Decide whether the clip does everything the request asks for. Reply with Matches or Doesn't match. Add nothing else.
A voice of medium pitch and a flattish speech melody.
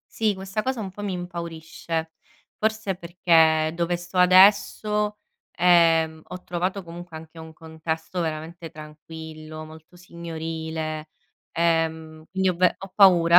Matches